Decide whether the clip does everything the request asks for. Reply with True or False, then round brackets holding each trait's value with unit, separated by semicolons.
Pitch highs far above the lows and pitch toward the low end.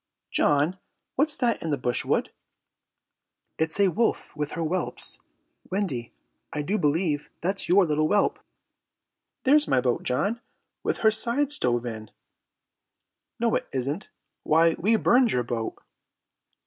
False (7.4 semitones; 165 Hz)